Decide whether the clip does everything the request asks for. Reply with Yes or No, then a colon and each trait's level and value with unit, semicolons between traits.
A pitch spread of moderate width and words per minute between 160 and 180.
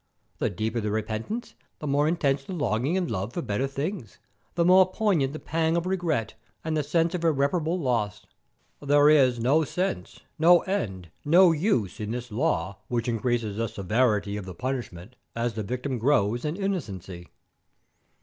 No: wide, 7.0 semitones; average, 170 wpm